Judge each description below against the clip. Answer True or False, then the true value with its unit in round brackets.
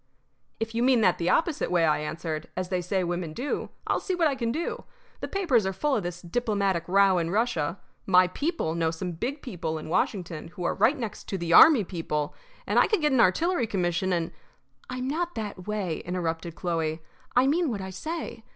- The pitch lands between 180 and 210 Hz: True (190 Hz)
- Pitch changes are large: True (6.6 semitones)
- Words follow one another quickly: True (215 wpm)